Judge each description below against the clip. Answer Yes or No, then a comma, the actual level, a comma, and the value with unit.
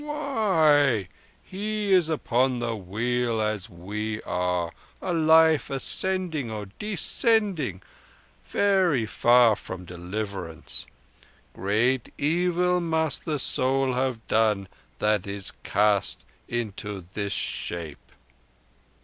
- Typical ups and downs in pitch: No, wide, 8.0 semitones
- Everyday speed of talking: No, slow, 90 wpm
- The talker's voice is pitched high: No, low, 120 Hz